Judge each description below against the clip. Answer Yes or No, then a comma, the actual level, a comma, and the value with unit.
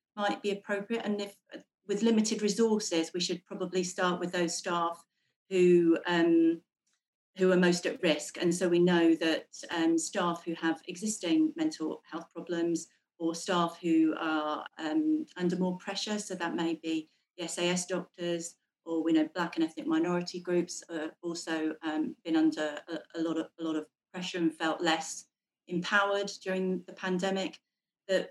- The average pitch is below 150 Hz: No, medium, 175 Hz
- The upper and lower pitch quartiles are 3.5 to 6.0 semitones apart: No, narrow, 2.6 semitones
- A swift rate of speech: No, average, 170 wpm